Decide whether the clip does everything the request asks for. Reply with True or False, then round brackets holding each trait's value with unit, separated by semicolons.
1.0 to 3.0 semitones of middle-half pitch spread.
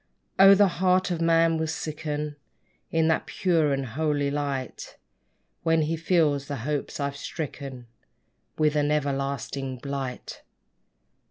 True (2.6 semitones)